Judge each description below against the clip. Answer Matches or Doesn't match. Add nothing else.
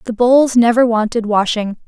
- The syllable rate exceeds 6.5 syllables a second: Doesn't match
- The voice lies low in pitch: Doesn't match